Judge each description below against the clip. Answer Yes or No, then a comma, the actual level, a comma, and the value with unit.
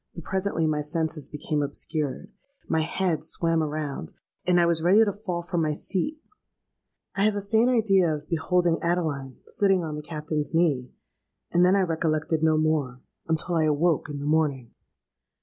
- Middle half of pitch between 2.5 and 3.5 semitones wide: Yes, average, 3.0 semitones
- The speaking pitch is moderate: Yes, medium, 160 Hz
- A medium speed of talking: Yes, average, 170 wpm